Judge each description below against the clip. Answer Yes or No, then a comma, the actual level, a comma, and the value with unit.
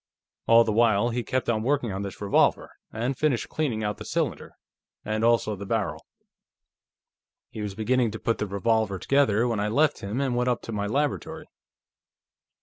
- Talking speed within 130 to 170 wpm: No, average, 180 wpm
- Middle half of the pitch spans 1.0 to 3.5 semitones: Yes, average, 3.0 semitones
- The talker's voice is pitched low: Yes, low, 115 Hz